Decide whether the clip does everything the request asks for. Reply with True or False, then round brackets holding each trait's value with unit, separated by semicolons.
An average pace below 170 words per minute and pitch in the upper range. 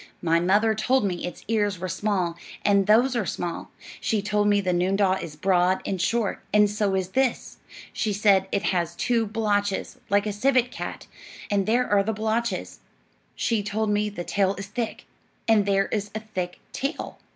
False (185 wpm; 205 Hz)